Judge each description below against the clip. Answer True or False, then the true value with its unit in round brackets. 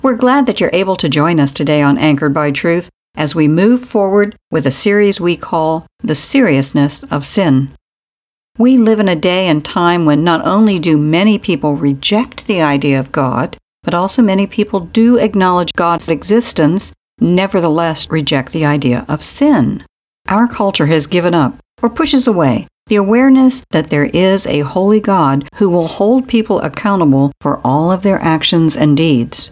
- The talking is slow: False (175 wpm)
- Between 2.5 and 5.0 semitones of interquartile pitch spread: False (5.6 semitones)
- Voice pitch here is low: False (175 Hz)